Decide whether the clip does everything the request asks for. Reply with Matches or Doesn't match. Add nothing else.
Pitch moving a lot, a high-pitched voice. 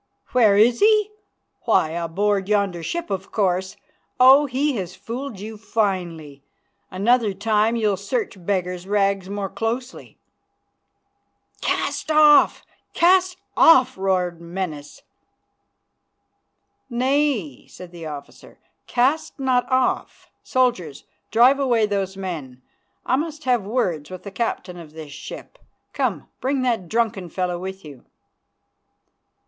Matches